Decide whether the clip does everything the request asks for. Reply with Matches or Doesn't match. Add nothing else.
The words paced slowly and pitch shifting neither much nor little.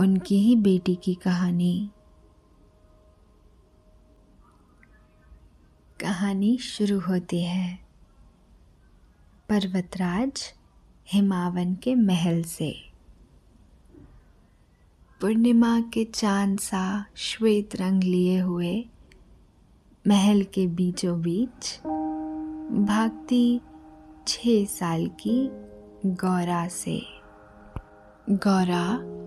Matches